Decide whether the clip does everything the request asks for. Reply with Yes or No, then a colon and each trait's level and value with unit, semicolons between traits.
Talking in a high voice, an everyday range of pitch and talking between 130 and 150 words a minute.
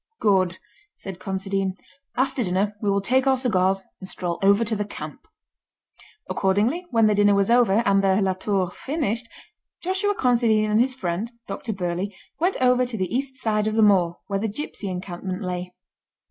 No: high, 205 Hz; average, 4.1 semitones; average, 175 wpm